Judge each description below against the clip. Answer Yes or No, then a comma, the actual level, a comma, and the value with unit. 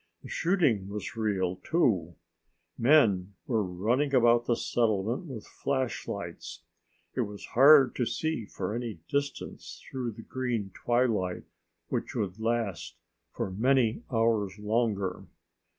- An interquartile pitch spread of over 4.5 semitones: No, average, 4.2 semitones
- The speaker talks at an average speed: No, slow, 120 wpm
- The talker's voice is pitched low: Yes, low, 115 Hz